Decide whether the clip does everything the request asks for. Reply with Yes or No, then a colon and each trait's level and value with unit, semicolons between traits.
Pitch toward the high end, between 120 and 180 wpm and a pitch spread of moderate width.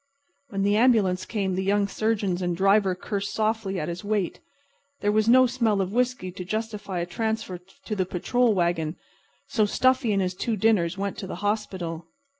No: high, 200 Hz; average, 190 wpm; average, 3.2 semitones